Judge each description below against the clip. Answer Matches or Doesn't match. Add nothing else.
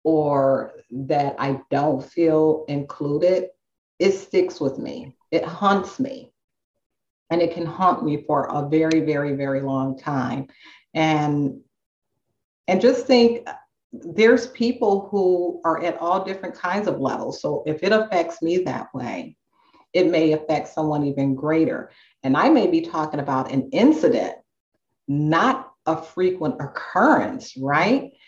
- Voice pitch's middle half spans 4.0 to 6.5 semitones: Matches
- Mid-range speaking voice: Matches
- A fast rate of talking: Doesn't match